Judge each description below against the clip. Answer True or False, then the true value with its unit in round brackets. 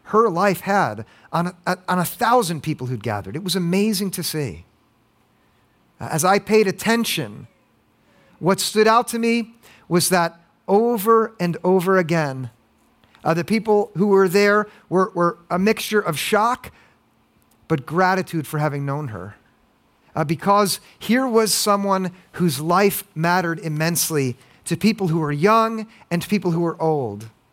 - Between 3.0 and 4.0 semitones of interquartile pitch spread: False (4.5 semitones)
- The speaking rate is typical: True (150 wpm)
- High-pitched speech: False (180 Hz)